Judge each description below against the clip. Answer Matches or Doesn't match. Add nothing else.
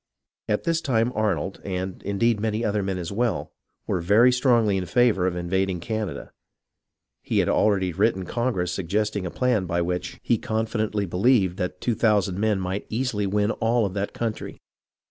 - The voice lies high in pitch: Doesn't match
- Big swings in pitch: Doesn't match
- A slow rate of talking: Doesn't match